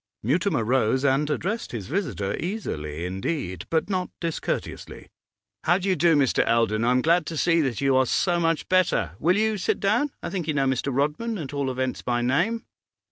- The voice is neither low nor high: Yes, medium, 150 Hz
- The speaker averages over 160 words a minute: Yes, average, 190 wpm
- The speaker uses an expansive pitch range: Yes, wide, 6.1 semitones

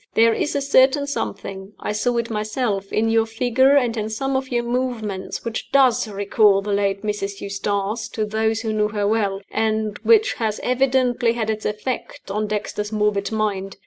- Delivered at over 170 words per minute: Yes, average, 180 wpm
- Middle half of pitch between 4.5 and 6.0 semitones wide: No, average, 2.8 semitones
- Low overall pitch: No, high, 220 Hz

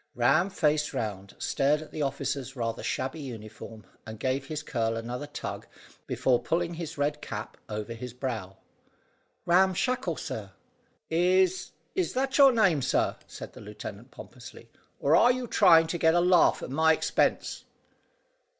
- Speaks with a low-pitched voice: No, medium, 145 Hz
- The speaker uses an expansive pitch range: Yes, wide, 6.9 semitones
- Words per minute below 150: No, average, 155 wpm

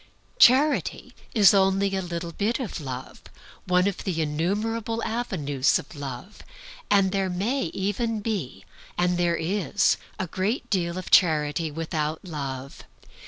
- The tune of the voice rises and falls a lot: No, average, 4.4 semitones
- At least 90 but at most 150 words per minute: Yes, slow, 135 wpm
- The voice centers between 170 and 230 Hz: Yes, medium, 185 Hz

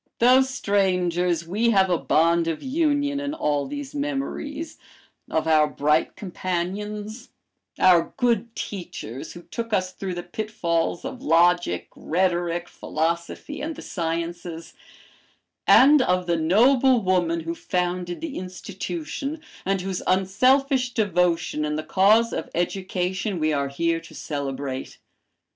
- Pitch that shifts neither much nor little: No, wide, 5.7 semitones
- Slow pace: Yes, slow, 130 wpm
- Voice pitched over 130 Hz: Yes, medium, 185 Hz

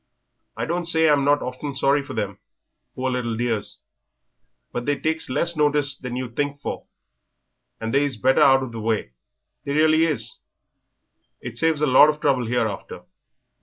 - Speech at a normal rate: Yes, average, 170 wpm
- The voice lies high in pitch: No, low, 135 Hz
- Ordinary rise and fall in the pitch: Yes, average, 3.5 semitones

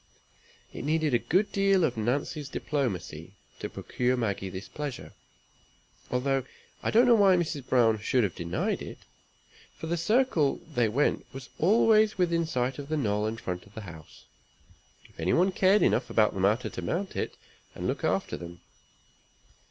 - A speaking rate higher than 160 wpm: Yes, average, 170 wpm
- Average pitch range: No, wide, 8.1 semitones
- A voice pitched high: No, low, 135 Hz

